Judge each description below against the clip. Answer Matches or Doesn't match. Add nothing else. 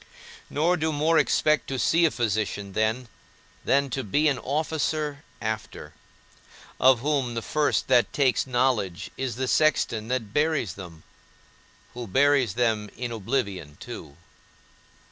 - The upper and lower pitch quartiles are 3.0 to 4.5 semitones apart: Doesn't match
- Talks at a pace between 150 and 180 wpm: Doesn't match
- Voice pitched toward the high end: Doesn't match